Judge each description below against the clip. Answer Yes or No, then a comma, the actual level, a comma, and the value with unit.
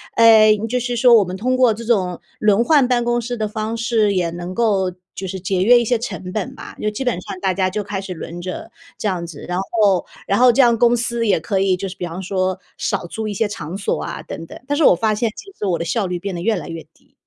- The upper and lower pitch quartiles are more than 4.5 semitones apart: No, average, 4.2 semitones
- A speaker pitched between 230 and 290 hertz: No, high, 210 Hz